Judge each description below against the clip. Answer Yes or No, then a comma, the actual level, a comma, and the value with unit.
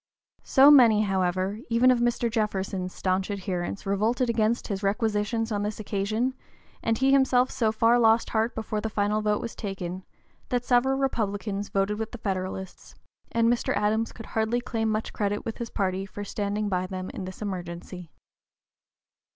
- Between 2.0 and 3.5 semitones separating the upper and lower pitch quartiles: Yes, average, 2.9 semitones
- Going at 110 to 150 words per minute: No, average, 165 wpm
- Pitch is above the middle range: Yes, high, 215 Hz